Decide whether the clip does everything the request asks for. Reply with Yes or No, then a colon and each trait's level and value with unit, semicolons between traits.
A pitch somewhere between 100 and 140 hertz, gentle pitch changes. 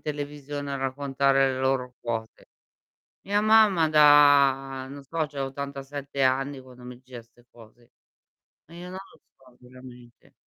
Yes: low, 135 Hz; narrow, 2.2 semitones